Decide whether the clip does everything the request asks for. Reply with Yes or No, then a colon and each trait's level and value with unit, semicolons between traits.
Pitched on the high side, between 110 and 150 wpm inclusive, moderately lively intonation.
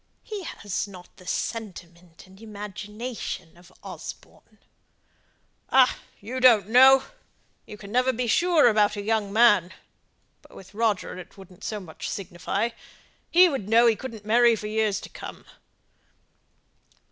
Yes: high, 215 Hz; average, 140 wpm; average, 3.6 semitones